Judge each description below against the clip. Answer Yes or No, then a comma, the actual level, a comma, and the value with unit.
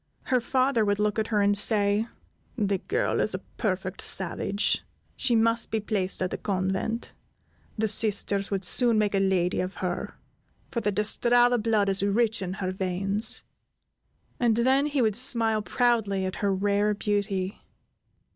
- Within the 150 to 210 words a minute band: Yes, average, 165 wpm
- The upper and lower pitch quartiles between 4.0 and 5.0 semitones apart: No, average, 2.8 semitones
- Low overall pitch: No, high, 210 Hz